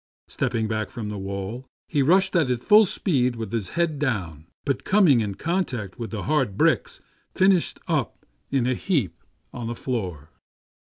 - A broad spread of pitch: Yes, wide, 6.7 semitones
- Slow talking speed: No, average, 175 wpm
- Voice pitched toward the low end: Yes, low, 120 Hz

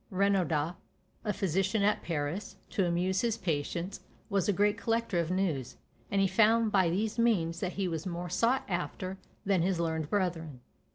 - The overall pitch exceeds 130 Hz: Yes, medium, 185 Hz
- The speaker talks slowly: No, average, 170 wpm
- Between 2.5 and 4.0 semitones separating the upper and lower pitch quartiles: Yes, average, 3.3 semitones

